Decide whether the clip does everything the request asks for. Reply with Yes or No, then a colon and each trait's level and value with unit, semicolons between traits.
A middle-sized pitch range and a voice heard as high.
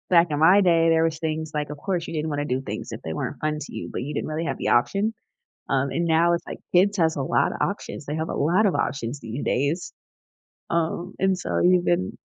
No: average, 3.2 semitones; medium, 160 Hz